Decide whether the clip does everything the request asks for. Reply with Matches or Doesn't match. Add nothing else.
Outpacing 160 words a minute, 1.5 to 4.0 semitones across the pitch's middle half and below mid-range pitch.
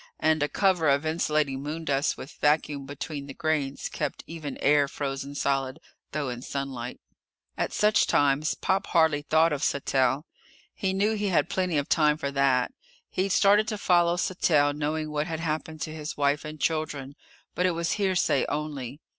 Doesn't match